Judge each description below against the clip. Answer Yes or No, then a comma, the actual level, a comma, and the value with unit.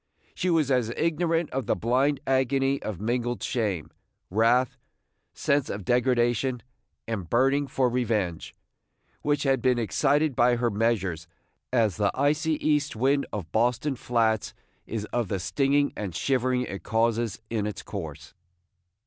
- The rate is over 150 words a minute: No, average, 140 wpm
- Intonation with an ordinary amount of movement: Yes, average, 3.9 semitones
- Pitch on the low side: Yes, low, 120 Hz